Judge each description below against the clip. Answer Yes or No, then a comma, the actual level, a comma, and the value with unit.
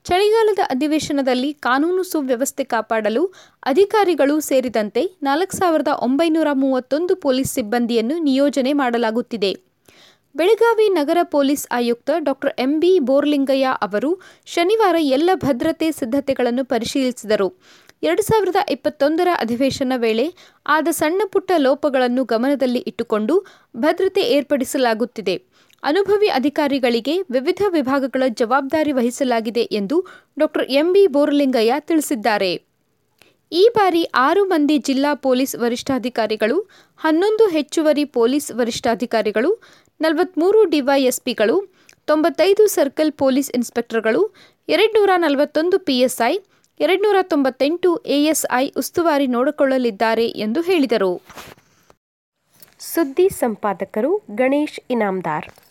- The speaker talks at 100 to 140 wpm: No, average, 90 wpm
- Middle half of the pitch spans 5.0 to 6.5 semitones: Yes, average, 5.3 semitones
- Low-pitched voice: No, very high, 280 Hz